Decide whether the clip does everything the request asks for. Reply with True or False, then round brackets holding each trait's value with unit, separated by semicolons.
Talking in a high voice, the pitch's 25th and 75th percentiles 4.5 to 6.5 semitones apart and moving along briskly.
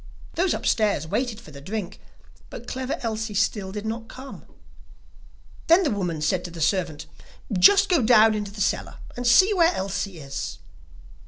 False (210 Hz; 4.8 semitones; 165 wpm)